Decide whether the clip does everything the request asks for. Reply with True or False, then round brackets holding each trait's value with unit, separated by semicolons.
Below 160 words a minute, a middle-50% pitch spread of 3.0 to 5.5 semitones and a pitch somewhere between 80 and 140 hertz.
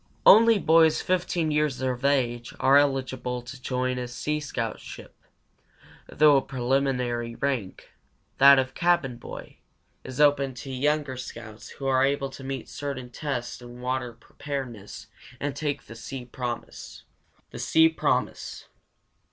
False (145 wpm; 2.6 semitones; 135 Hz)